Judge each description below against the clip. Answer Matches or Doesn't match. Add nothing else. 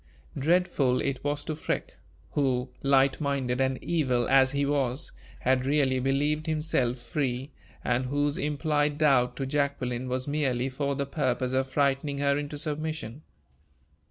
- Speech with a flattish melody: Matches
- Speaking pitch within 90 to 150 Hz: Matches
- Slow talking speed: Doesn't match